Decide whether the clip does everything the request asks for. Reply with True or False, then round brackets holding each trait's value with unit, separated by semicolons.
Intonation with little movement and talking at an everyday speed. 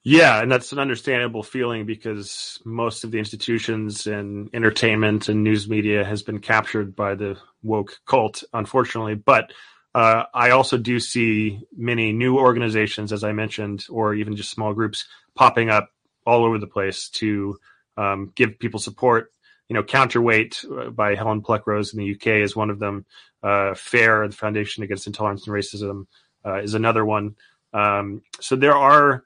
True (1.9 semitones; 170 wpm)